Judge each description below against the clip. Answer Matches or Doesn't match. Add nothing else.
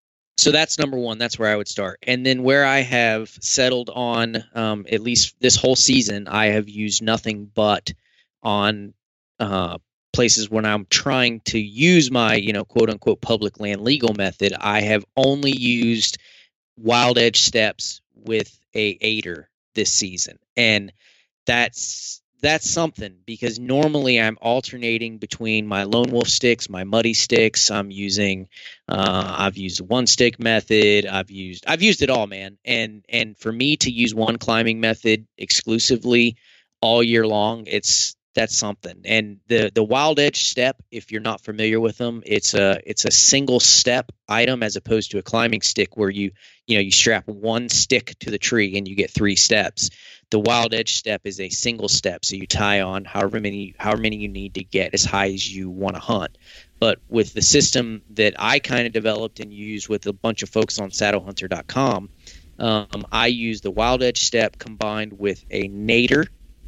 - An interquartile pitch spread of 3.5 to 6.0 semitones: Doesn't match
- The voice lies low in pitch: Matches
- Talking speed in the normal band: Matches